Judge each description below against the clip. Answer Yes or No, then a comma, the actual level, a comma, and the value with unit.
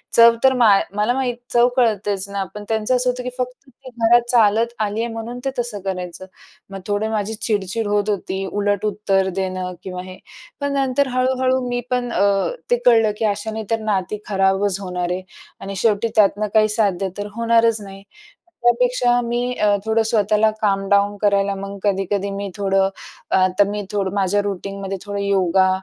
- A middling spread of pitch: Yes, average, 3.0 semitones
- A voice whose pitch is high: Yes, high, 205 Hz